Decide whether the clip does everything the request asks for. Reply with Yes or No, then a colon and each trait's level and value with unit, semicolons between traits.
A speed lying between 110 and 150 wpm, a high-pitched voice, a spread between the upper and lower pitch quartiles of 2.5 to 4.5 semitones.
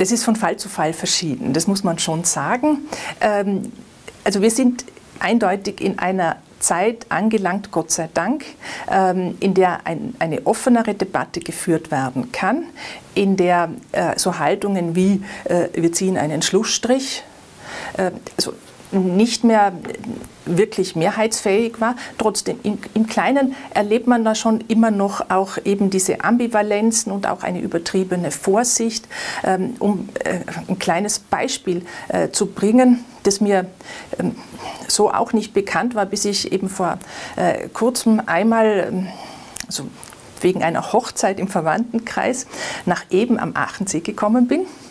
Yes: slow, 125 wpm; high, 205 Hz; average, 3.7 semitones